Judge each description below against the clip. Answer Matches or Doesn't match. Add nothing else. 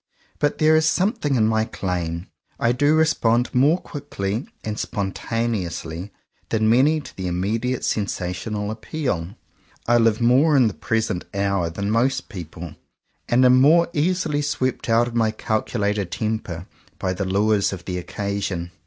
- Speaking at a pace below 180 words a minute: Matches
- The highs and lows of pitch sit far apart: Doesn't match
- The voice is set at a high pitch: Doesn't match